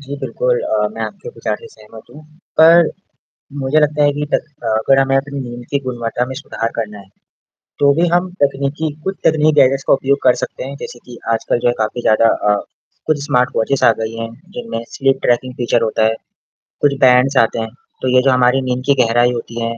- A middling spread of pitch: Yes, average, 3.1 semitones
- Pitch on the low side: Yes, low, 130 Hz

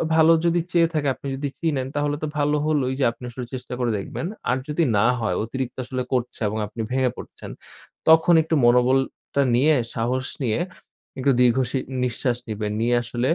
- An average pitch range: Yes, average, 3.4 semitones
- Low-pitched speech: Yes, low, 130 Hz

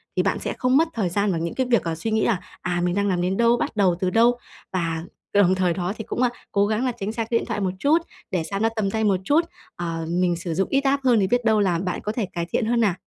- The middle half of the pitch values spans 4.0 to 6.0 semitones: Yes, average, 4.6 semitones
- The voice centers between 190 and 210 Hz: Yes, high, 200 Hz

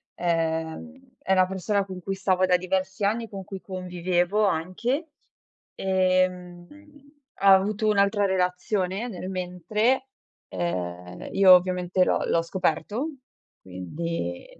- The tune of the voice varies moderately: No, narrow, 2.2 semitones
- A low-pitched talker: No, medium, 185 Hz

